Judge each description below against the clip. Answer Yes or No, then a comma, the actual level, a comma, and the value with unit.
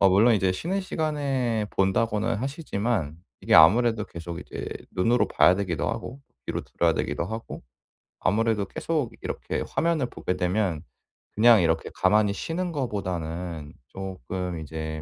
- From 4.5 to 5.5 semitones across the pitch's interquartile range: Yes, average, 5.2 semitones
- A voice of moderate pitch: No, low, 100 Hz